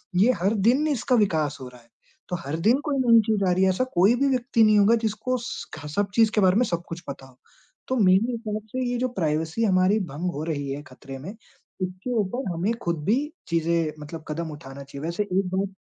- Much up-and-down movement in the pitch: Yes, wide, 6.2 semitones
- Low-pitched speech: No, medium, 185 Hz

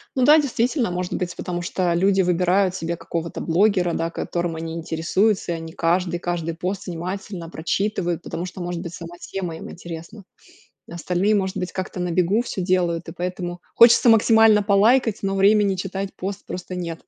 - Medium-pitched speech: Yes, medium, 180 Hz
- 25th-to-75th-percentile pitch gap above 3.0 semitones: No, narrow, 2.6 semitones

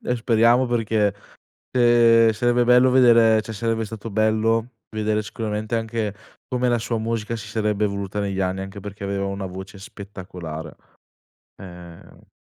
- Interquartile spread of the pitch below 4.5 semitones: Yes, narrow, 2.6 semitones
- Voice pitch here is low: Yes, low, 110 Hz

